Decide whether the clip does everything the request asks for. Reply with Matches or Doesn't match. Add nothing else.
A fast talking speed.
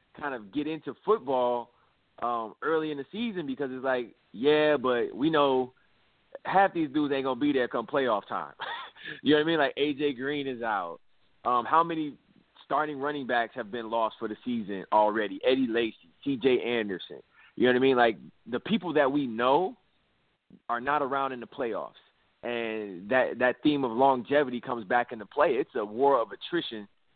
Doesn't match